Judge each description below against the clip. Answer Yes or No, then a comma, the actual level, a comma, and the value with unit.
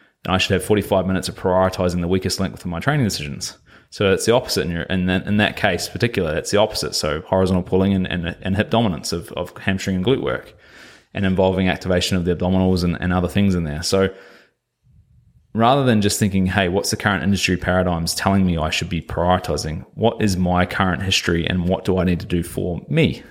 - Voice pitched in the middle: No, very low, 95 Hz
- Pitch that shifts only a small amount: Yes, narrow, 1.4 semitones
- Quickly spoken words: Yes, fast, 225 wpm